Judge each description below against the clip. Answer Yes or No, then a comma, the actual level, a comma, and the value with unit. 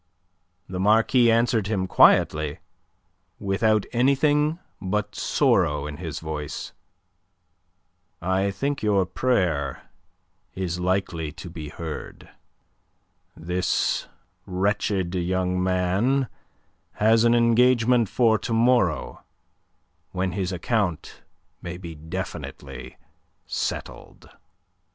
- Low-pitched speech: Yes, very low, 95 Hz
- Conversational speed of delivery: No, slow, 90 wpm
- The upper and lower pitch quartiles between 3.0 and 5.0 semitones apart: Yes, average, 4.5 semitones